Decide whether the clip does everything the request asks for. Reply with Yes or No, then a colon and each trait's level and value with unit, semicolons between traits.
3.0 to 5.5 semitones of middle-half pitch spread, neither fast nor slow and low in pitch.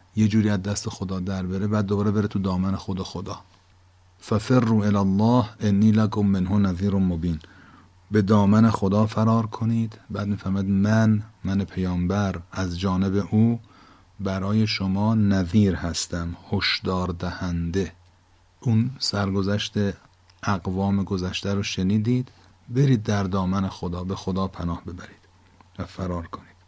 No: narrow, 2.4 semitones; average, 130 wpm; low, 100 Hz